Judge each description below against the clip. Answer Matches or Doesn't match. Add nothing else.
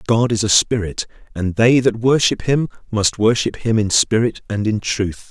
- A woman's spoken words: Doesn't match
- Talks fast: Doesn't match